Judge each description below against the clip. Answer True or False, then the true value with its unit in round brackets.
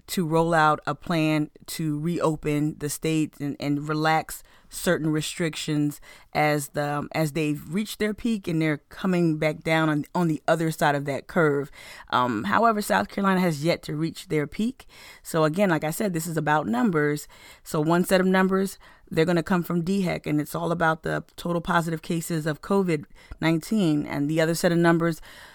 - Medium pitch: True (160 Hz)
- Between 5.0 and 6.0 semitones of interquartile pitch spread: False (2.5 semitones)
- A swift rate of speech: False (190 wpm)